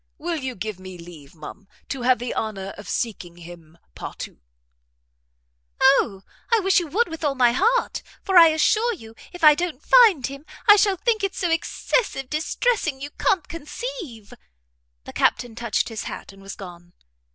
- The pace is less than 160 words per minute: No, average, 175 wpm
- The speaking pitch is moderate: No, very high, 275 Hz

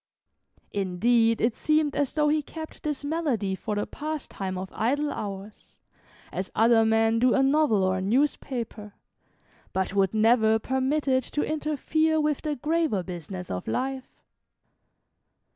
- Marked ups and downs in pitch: Yes, wide, 6.4 semitones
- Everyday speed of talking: Yes, average, 145 wpm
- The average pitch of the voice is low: No, high, 240 Hz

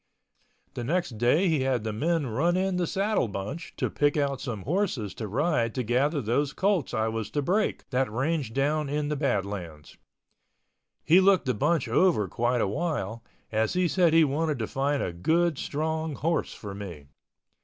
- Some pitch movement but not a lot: No, wide, 6.4 semitones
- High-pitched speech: No, medium, 140 Hz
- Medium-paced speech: Yes, average, 185 wpm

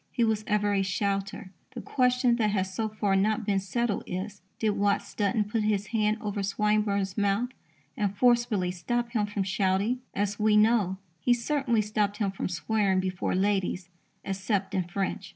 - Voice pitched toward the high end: Yes, high, 205 Hz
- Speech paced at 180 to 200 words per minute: No, average, 170 wpm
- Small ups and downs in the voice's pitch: Yes, narrow, 2.2 semitones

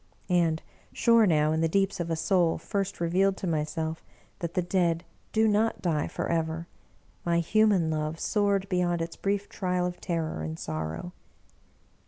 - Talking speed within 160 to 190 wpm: Yes, average, 170 wpm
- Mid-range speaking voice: Yes, medium, 170 Hz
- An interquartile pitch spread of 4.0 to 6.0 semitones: No, average, 3.3 semitones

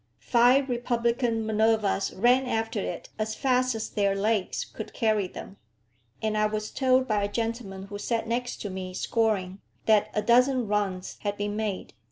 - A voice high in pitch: Yes, high, 220 Hz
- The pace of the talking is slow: No, average, 170 wpm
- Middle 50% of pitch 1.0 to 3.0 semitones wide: Yes, average, 2.7 semitones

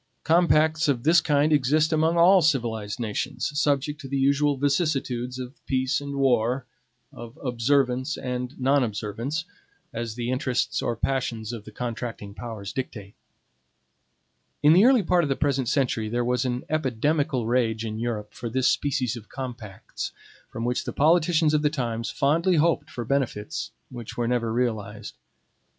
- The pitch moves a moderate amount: Yes, average, 4.0 semitones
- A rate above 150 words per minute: Yes, average, 160 wpm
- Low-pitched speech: Yes, low, 130 Hz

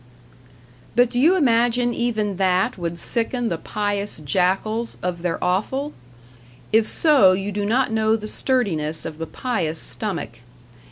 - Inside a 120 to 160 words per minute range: Yes, average, 145 wpm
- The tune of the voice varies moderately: Yes, average, 5.0 semitones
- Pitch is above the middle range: Yes, high, 210 Hz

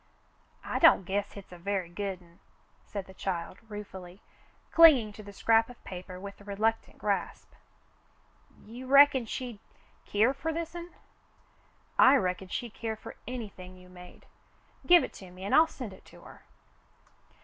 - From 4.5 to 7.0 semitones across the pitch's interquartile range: Yes, average, 4.9 semitones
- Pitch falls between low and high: No, high, 205 Hz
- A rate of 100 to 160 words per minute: Yes, average, 150 wpm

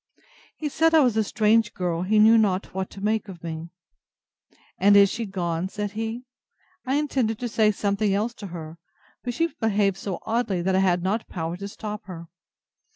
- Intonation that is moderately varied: Yes, average, 3.1 semitones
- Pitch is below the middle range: No, high, 205 Hz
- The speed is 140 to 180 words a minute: No, average, 195 wpm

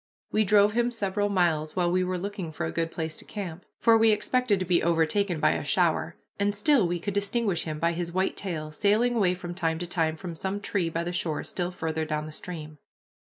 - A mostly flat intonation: No, average, 3.8 semitones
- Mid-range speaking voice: Yes, medium, 180 Hz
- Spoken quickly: Yes, fast, 230 wpm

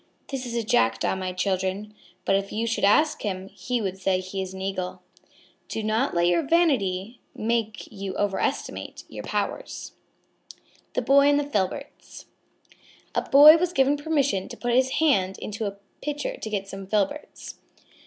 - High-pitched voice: Yes, high, 215 Hz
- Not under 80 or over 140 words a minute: No, average, 165 wpm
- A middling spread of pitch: No, wide, 6.3 semitones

